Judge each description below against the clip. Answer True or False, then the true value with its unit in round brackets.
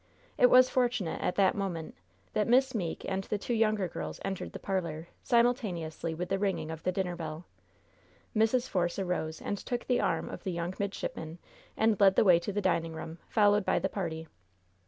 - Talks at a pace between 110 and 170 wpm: False (195 wpm)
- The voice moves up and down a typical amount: True (4.2 semitones)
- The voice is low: False (190 Hz)